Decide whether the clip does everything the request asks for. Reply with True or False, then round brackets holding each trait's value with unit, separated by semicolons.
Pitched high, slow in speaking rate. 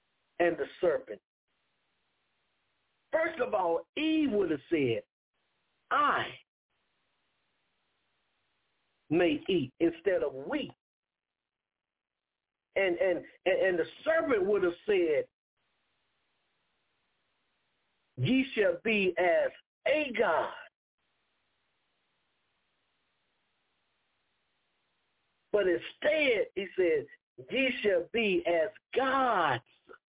True (300 Hz; 80 wpm)